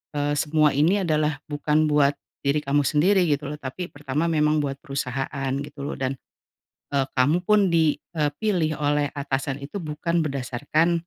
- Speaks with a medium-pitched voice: Yes, medium, 150 Hz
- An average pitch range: No, narrow, 2.1 semitones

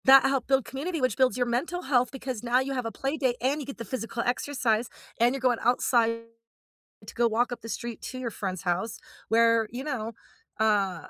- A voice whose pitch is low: No, high, 245 Hz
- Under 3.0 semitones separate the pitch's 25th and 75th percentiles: Yes, narrow, 2.6 semitones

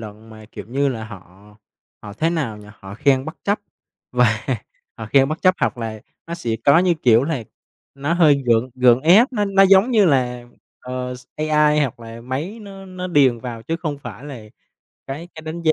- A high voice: No, low, 135 Hz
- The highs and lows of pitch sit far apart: Yes, wide, 6.0 semitones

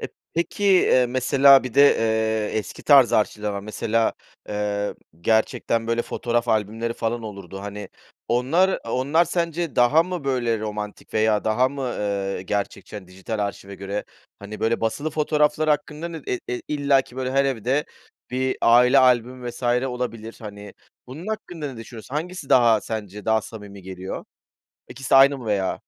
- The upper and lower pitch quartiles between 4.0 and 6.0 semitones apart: Yes, average, 4.6 semitones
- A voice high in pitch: No, low, 120 Hz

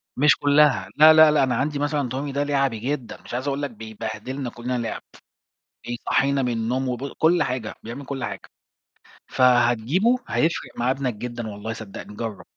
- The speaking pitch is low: Yes, low, 130 Hz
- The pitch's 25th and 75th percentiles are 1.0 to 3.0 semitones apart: No, average, 3.5 semitones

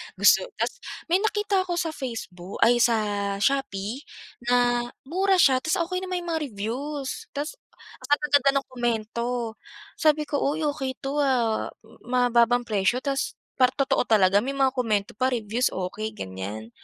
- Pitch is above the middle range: Yes, very high, 255 Hz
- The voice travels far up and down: No, average, 4.6 semitones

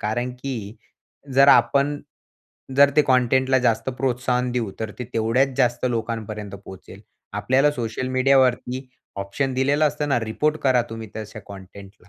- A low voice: Yes, low, 125 Hz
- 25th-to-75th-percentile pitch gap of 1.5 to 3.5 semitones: Yes, average, 3.1 semitones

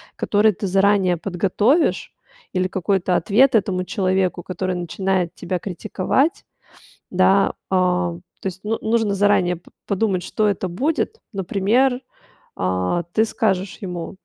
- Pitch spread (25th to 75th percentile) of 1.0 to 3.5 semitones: Yes, narrow, 2.5 semitones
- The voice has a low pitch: No, high, 190 Hz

